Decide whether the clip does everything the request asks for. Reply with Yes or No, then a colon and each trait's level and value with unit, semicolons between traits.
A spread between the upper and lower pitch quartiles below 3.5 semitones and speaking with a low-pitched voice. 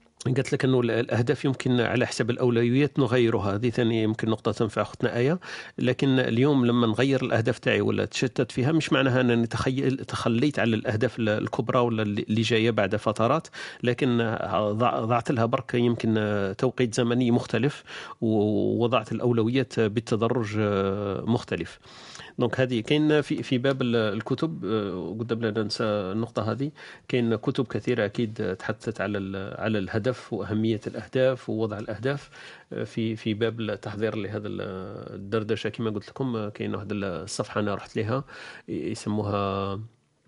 Yes: narrow, 2.6 semitones; low, 115 Hz